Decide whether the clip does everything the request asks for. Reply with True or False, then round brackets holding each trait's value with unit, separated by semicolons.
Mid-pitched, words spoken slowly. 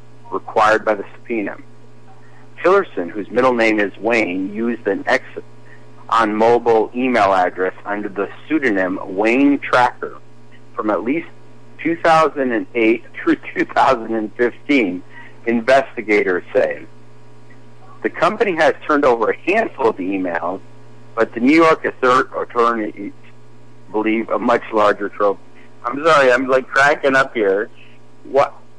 False (105 Hz; 120 wpm)